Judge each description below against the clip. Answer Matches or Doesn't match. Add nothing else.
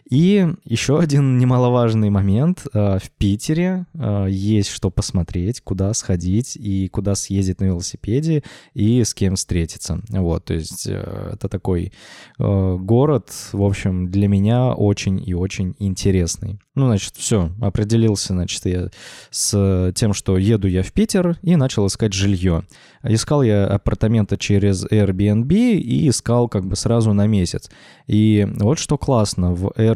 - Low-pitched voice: Matches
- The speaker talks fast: Doesn't match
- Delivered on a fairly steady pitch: Doesn't match